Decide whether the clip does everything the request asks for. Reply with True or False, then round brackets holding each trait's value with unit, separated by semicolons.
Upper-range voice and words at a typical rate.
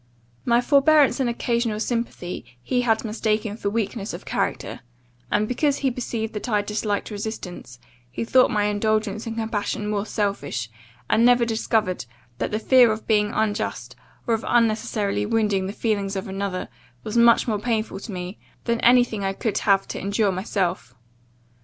True (215 Hz; 165 wpm)